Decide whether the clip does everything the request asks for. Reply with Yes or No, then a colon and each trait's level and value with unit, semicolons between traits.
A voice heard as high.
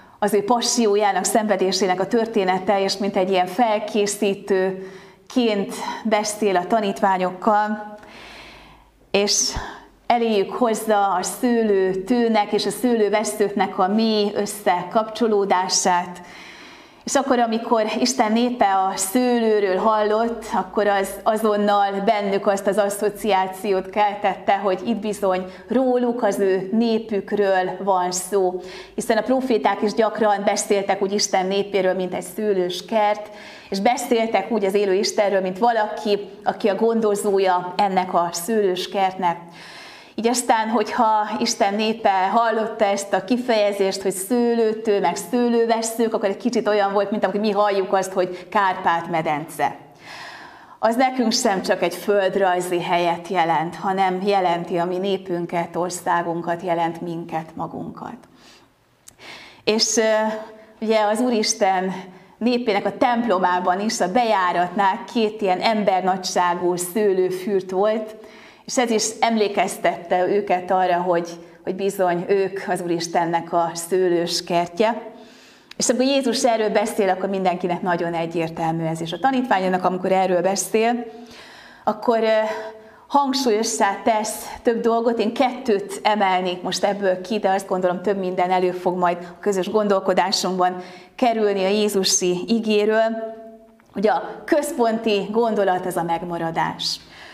Yes: high, 200 Hz